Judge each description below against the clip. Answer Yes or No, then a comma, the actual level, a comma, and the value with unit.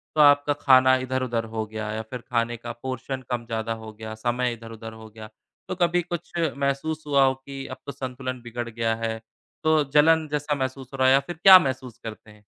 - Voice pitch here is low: Yes, low, 130 Hz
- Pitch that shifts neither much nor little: Yes, average, 3.9 semitones